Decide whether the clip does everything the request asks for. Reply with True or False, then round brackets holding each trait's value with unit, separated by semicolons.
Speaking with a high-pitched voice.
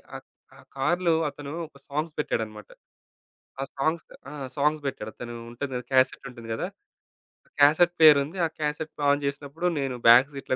False (140 Hz)